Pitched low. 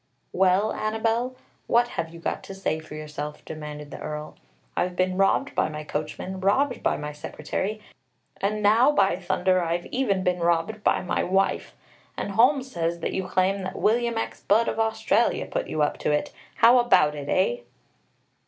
No: medium, 185 Hz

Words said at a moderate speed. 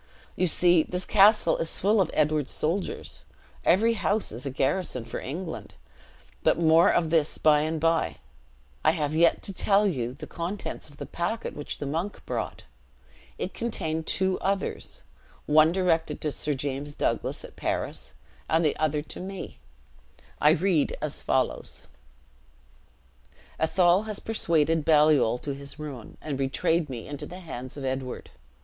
Yes: average, 155 wpm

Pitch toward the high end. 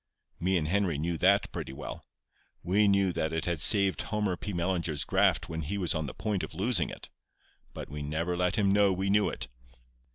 No: very low, 90 Hz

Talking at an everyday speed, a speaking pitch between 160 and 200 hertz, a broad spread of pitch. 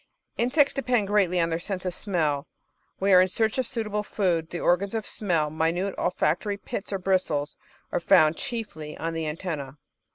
No: average, 185 wpm; medium, 185 Hz; average, 4.2 semitones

